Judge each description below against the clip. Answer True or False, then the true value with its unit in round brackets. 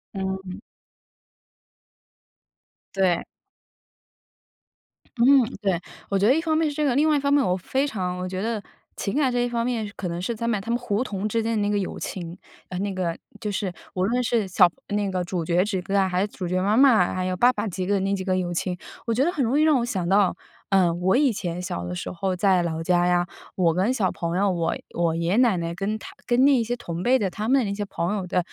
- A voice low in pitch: False (195 Hz)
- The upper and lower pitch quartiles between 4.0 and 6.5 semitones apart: True (4.5 semitones)